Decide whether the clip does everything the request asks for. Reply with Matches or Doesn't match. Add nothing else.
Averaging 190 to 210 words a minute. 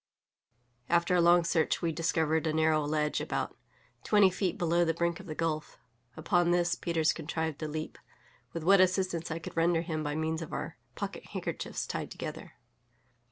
Doesn't match